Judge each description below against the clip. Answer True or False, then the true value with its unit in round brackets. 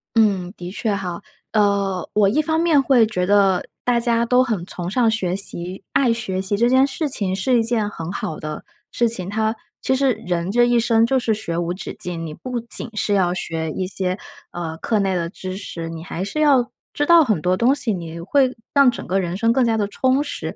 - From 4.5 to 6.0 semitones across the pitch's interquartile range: True (4.8 semitones)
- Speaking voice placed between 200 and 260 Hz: True (205 Hz)